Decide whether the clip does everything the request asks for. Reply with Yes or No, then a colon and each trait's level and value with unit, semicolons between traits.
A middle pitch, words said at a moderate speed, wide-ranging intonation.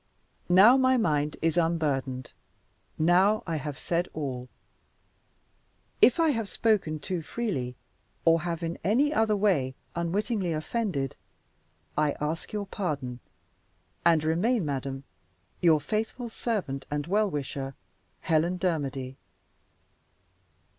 No: medium, 165 Hz; slow, 115 wpm; wide, 6.2 semitones